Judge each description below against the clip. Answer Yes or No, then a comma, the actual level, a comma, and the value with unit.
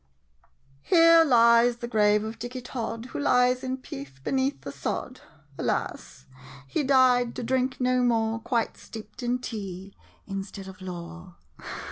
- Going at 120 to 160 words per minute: Yes, average, 145 wpm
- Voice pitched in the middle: No, high, 235 Hz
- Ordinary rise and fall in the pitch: Yes, average, 4.0 semitones